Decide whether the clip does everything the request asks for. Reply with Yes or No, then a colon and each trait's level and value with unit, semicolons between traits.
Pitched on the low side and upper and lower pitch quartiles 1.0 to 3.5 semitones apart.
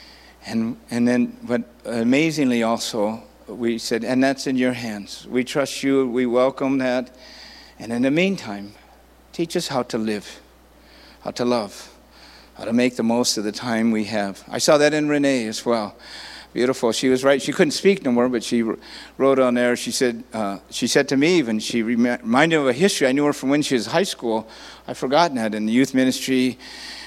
Yes: low, 125 Hz; average, 3.0 semitones